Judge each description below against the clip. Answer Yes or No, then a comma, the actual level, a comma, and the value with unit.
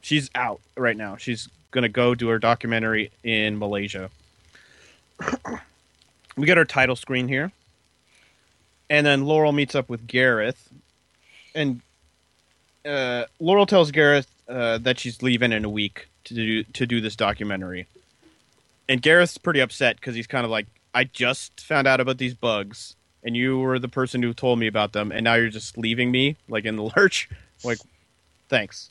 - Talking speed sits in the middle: Yes, average, 170 wpm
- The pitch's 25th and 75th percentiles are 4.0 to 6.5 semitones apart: No, average, 3.4 semitones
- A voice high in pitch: No, low, 120 Hz